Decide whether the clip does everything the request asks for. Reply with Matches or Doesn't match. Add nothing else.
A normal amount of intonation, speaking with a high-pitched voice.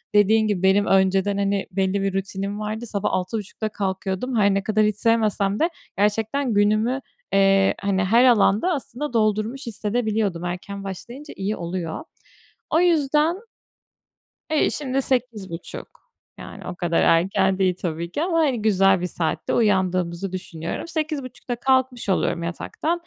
Matches